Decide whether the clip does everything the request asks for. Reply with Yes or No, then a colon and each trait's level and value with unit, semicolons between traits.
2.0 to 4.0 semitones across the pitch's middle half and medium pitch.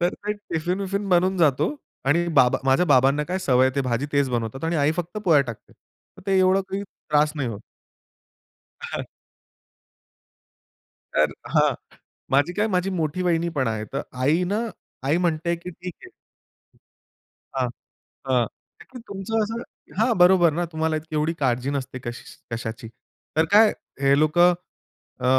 No: average, 5.3 semitones; medium, 160 Hz